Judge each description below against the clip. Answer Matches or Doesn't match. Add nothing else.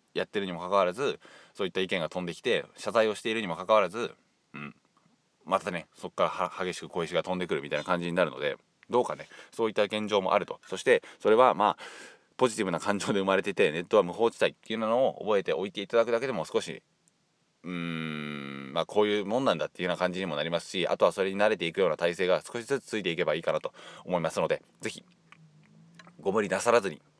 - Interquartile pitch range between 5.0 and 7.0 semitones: Doesn't match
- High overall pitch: Doesn't match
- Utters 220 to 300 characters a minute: Doesn't match